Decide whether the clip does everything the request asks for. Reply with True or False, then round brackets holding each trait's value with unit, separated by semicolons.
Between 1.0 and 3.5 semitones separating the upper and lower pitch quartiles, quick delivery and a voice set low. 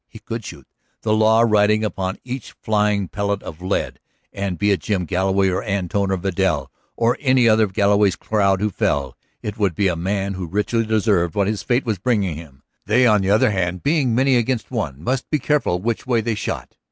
True (2.9 semitones; 210 wpm; 105 Hz)